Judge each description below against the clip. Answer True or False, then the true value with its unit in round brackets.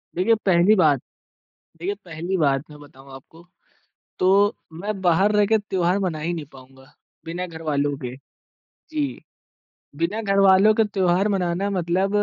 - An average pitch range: True (4.0 semitones)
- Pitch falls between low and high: True (180 Hz)